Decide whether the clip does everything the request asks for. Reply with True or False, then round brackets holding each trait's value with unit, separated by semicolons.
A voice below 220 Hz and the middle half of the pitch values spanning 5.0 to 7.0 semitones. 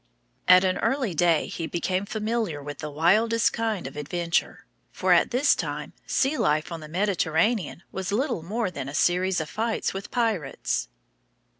True (185 Hz; 5.5 semitones)